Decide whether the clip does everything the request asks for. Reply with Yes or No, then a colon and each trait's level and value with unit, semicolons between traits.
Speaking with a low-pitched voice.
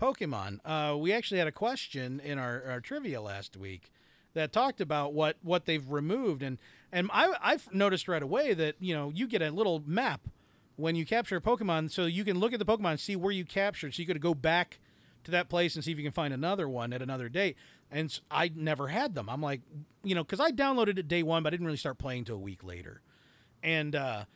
No: medium, 160 Hz